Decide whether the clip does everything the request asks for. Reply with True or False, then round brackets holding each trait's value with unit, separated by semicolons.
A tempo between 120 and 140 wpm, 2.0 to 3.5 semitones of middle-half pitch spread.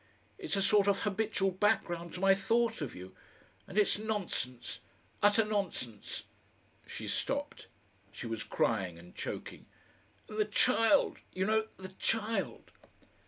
False (135 wpm; 4.0 semitones)